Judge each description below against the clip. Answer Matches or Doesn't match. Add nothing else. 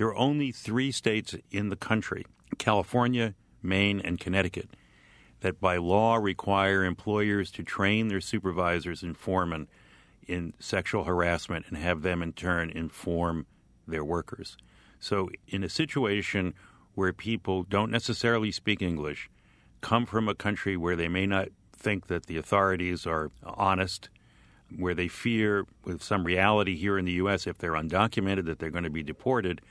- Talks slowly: Doesn't match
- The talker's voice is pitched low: Matches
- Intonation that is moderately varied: Matches